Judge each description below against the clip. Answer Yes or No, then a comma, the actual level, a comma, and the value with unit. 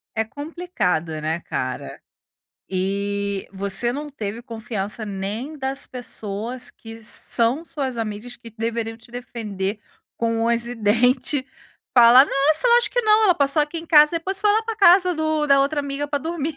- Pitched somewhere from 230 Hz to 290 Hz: Yes, high, 245 Hz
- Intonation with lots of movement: Yes, wide, 5.7 semitones